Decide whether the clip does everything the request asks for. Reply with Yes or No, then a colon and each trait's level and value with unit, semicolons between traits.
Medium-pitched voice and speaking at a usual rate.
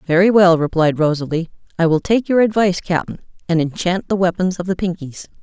Yes: medium, 180 Hz; average, 190 wpm